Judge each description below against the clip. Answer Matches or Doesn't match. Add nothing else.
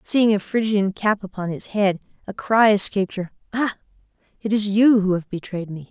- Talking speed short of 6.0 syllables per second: Matches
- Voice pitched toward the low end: Doesn't match